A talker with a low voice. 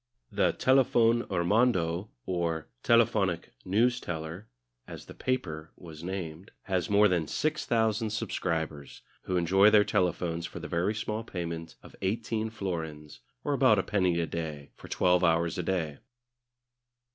Yes: very low, 90 Hz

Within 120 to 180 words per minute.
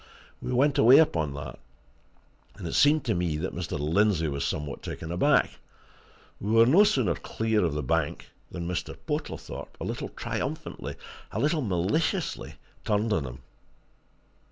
Yes: average, 155 wpm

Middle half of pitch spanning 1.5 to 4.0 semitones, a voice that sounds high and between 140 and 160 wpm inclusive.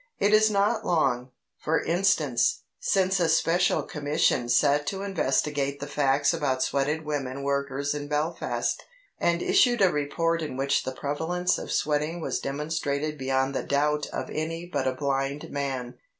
No: average, 3.2 semitones; medium, 150 Hz; average, 155 wpm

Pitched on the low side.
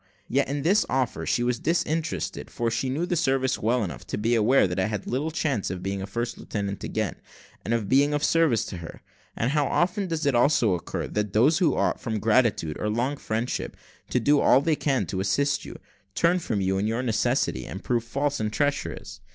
Yes: low, 125 Hz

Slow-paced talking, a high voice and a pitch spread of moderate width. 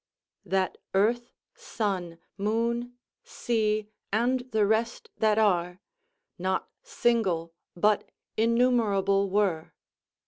Yes: slow, 90 wpm; high, 215 Hz; average, 3.4 semitones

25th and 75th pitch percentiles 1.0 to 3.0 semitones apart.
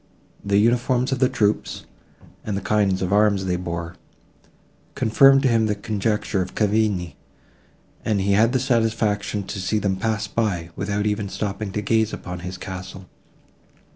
Yes: narrow, 2.6 semitones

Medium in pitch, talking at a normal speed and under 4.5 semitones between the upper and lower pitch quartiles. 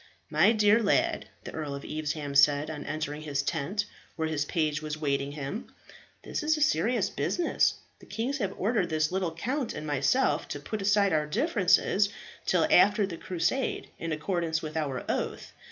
No: medium, 165 Hz; average, 175 wpm; wide, 5.5 semitones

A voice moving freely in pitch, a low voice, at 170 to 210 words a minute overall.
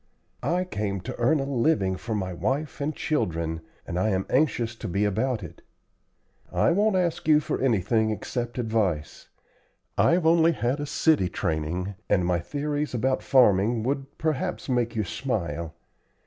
No: wide, 7.3 semitones; low, 120 Hz; average, 160 wpm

